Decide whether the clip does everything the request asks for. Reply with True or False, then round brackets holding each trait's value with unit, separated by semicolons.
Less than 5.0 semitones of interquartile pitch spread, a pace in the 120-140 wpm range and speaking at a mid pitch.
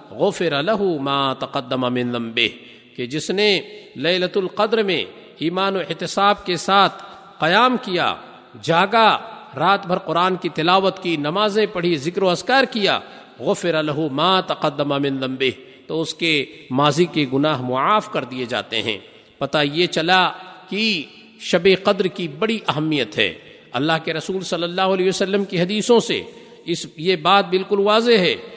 False (4.6 semitones; 160 wpm; 180 Hz)